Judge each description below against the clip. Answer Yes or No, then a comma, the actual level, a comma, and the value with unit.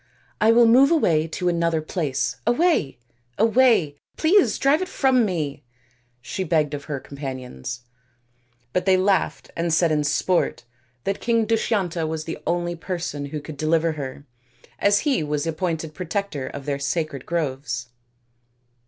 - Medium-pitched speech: Yes, medium, 165 Hz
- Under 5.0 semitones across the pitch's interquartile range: No, wide, 5.5 semitones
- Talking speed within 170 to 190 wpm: No, average, 155 wpm